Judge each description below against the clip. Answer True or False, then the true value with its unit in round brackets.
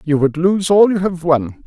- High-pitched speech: False (170 Hz)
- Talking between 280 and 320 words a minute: False (250 wpm)